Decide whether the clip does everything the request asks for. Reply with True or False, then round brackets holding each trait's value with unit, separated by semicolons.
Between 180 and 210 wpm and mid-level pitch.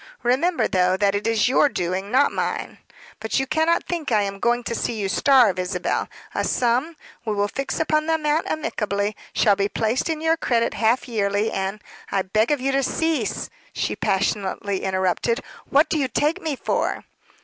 False (190 wpm; 230 Hz)